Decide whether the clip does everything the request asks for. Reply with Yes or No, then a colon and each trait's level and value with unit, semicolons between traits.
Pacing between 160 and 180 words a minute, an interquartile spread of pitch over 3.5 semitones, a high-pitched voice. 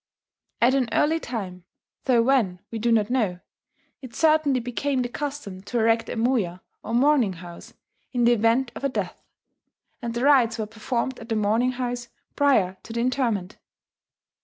No: average, 170 wpm; average, 3.1 semitones; high, 235 Hz